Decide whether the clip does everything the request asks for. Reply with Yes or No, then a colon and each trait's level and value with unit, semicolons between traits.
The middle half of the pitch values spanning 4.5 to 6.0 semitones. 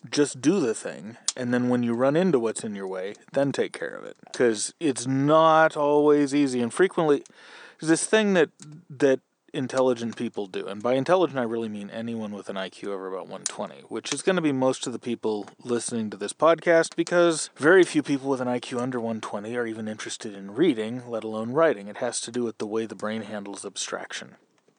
Yes: wide, 5.5 semitones